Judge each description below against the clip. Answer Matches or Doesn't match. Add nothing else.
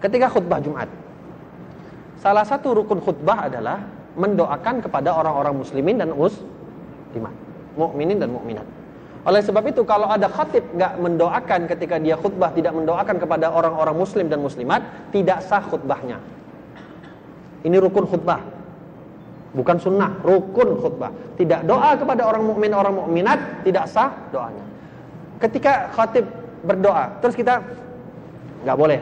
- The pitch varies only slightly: Doesn't match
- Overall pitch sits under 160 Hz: Doesn't match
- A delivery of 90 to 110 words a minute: Doesn't match